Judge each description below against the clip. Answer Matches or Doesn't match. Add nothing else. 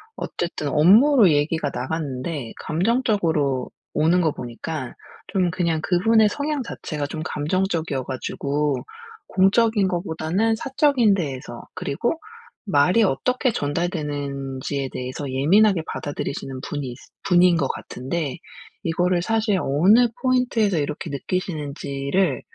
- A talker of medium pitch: Matches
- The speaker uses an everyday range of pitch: Doesn't match